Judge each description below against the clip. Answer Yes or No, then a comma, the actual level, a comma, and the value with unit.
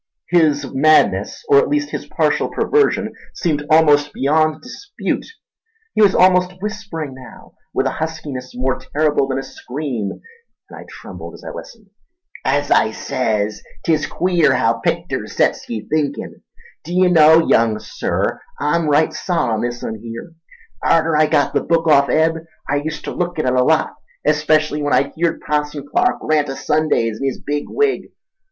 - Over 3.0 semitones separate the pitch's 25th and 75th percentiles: Yes, average, 3.5 semitones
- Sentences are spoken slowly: No, average, 165 wpm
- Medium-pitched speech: Yes, medium, 150 Hz